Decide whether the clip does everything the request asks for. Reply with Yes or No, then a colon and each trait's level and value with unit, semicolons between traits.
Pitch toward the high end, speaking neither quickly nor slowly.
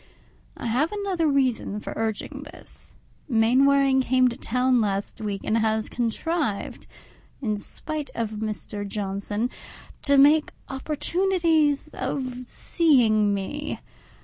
No: very high, 250 Hz; slow, 115 wpm